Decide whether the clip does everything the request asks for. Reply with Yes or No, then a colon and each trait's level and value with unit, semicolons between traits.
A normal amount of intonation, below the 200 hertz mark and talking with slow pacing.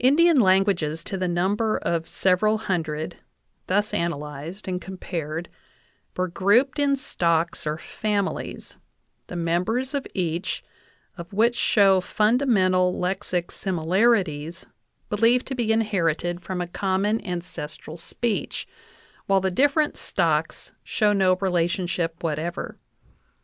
Yes: average, 3.9 semitones; medium, 185 Hz; slow, 115 wpm